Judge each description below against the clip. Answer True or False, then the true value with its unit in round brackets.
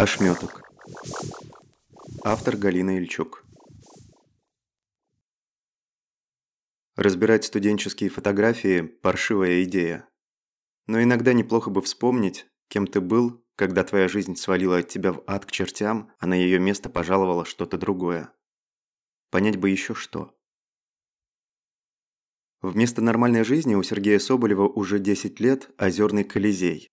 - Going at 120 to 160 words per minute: False (110 wpm)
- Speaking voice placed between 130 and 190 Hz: False (100 Hz)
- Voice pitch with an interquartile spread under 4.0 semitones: True (3.0 semitones)